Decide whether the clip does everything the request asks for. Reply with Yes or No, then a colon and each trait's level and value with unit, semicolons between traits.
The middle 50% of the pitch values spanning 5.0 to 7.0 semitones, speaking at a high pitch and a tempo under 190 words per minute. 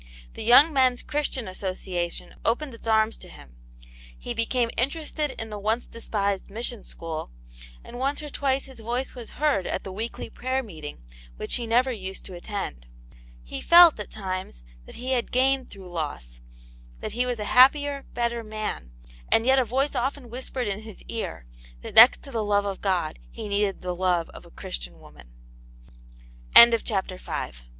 Yes: average, 5.3 semitones; high, 225 Hz; average, 175 wpm